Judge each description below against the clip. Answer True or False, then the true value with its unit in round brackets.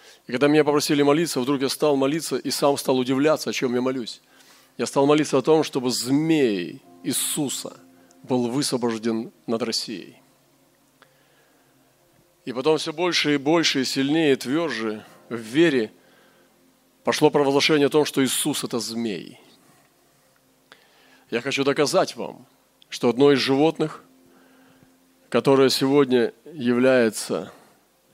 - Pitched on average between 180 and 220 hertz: False (135 Hz)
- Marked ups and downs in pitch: False (3.9 semitones)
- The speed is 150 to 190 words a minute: False (130 wpm)